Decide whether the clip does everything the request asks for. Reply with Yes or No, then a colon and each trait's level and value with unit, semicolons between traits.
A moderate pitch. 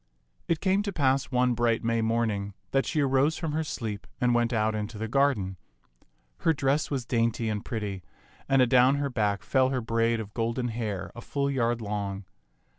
No: low, 120 Hz